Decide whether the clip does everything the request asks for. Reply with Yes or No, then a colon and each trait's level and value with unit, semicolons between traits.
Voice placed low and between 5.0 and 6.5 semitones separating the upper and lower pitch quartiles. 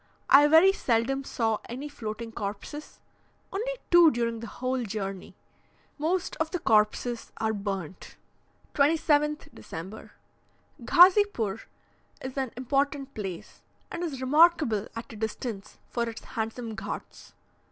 No: high, 245 Hz; wide, 5.4 semitones